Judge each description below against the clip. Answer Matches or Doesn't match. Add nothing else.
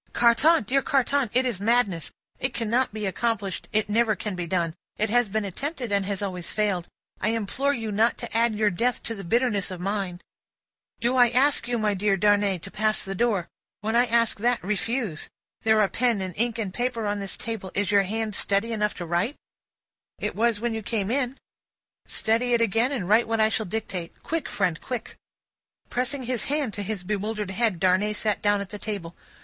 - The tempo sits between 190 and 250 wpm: Matches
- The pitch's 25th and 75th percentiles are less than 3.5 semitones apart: Matches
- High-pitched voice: Matches